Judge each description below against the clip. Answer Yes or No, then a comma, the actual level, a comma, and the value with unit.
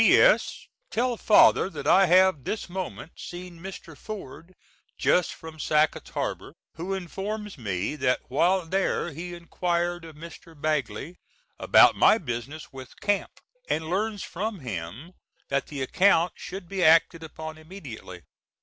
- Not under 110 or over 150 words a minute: Yes, average, 140 wpm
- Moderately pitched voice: Yes, medium, 170 Hz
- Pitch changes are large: No, average, 3.9 semitones